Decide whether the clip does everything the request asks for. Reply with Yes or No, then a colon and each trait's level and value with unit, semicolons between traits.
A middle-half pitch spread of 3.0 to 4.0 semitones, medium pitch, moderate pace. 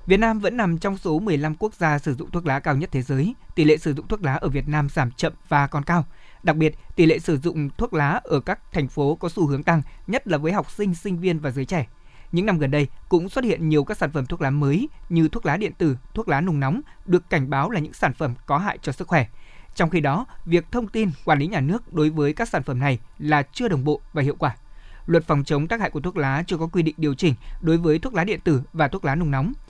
No: average, 3.5 semitones; medium, 155 Hz; fast, 285 wpm